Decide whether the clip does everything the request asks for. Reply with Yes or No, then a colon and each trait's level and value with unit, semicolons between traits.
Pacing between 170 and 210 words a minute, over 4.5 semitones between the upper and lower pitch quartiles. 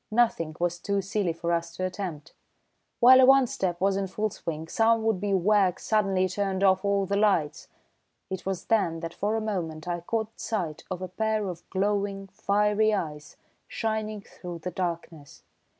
No: average, 180 wpm; average, 3.5 semitones